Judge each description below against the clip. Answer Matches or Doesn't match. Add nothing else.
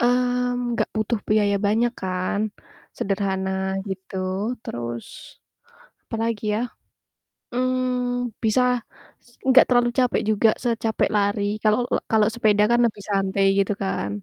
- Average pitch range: Matches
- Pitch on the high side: Matches